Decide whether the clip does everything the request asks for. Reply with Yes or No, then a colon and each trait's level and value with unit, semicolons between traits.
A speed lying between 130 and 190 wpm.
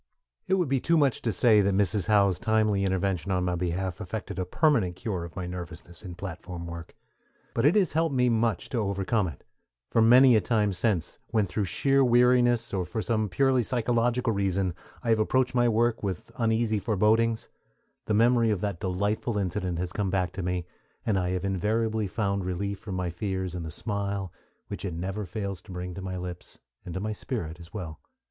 No: average, 200 wpm